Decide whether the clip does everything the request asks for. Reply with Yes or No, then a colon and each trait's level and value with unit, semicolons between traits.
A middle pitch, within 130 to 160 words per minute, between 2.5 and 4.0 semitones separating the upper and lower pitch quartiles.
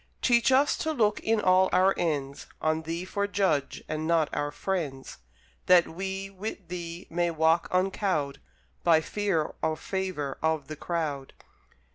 Yes: medium, 170 Hz; average, 150 wpm; average, 3.5 semitones